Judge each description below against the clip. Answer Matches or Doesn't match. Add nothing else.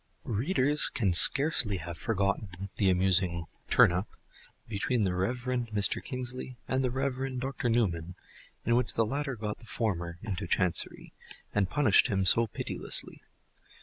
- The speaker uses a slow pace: Doesn't match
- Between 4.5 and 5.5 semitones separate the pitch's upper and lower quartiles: Matches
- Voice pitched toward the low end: Matches